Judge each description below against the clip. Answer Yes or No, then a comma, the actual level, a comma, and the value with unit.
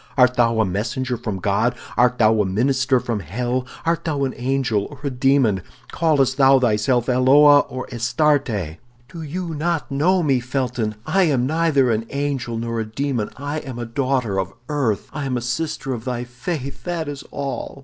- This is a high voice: No, low, 130 Hz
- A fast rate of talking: No, average, 185 wpm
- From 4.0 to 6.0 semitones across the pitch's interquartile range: No, average, 3.5 semitones